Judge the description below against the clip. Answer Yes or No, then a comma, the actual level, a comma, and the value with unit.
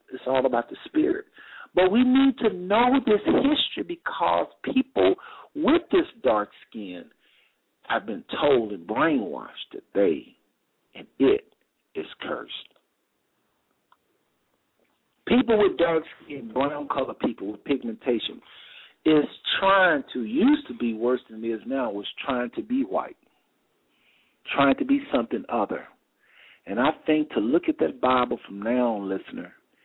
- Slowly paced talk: No, average, 145 wpm